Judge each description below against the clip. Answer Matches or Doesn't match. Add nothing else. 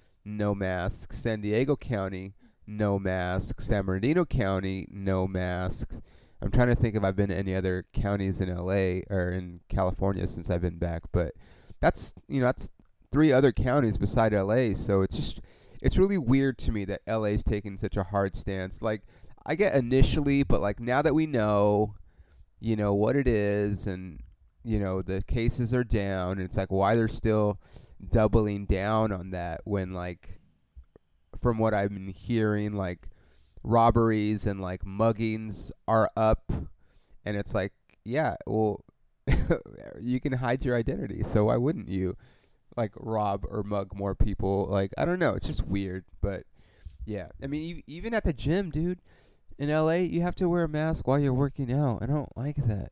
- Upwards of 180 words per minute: Doesn't match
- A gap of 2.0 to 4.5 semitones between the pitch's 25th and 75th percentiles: Matches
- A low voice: Matches